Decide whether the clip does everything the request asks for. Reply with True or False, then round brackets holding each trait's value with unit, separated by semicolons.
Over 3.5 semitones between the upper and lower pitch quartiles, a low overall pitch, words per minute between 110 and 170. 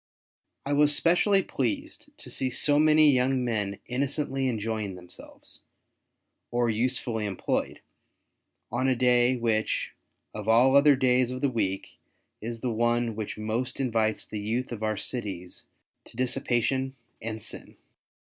False (3.2 semitones; 120 Hz; 135 wpm)